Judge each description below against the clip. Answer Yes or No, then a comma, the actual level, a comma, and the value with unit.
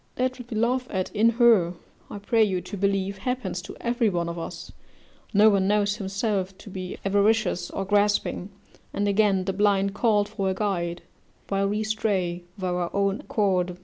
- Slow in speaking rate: No, average, 180 wpm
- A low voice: No, high, 200 Hz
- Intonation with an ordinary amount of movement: No, narrow, 2.3 semitones